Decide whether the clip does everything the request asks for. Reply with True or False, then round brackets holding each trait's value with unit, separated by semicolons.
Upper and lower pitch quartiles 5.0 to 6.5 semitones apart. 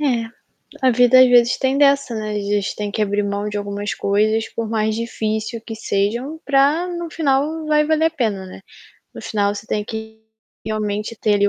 False (4.6 semitones)